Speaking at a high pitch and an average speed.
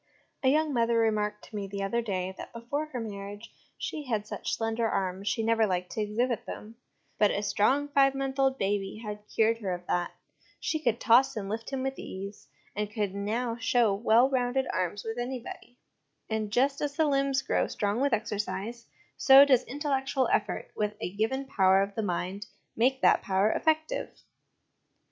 Yes: high, 225 Hz; average, 185 wpm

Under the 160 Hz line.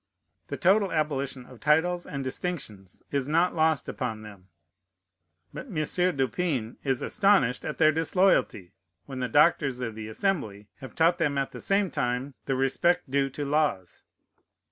Yes: medium, 140 Hz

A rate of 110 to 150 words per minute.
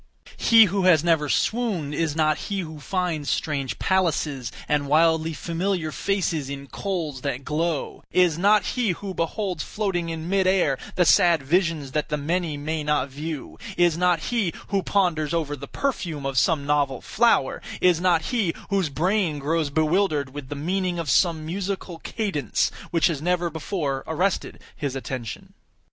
No: average, 165 wpm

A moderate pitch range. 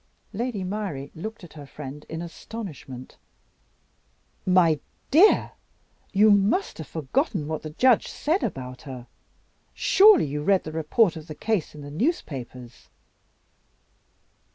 No: wide, 6.8 semitones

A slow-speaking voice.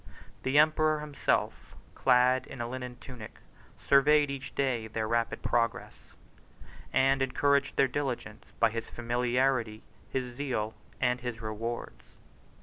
Yes: slow, 125 wpm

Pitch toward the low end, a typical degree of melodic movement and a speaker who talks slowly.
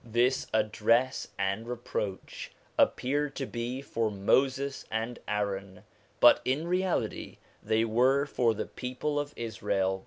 Yes: low, 120 Hz; average, 4.1 semitones; slow, 125 wpm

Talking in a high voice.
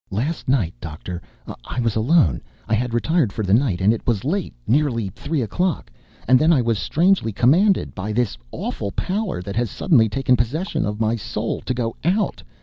No: low, 120 Hz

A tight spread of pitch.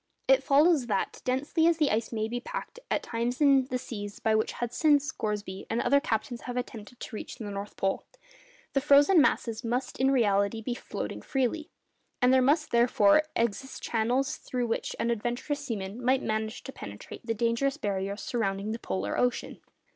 No: average, 4.0 semitones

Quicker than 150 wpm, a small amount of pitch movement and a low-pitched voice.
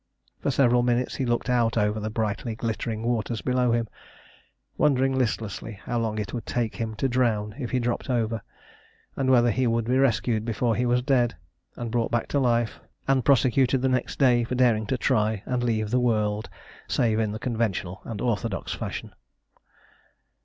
Yes: average, 180 wpm; narrow, 2.3 semitones; low, 120 Hz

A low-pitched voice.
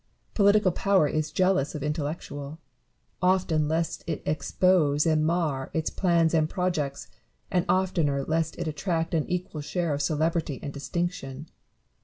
No: medium, 160 Hz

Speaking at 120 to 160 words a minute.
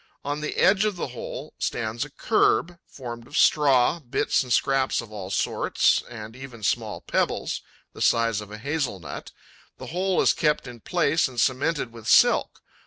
No: average, 175 wpm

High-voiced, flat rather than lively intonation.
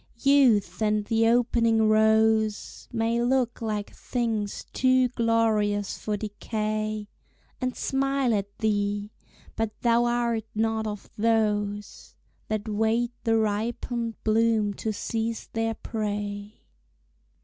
Yes: high, 220 Hz; narrow, 1.7 semitones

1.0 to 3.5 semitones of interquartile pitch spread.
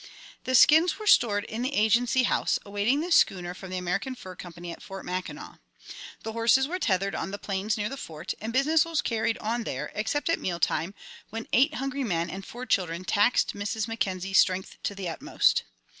No: wide, 5.4 semitones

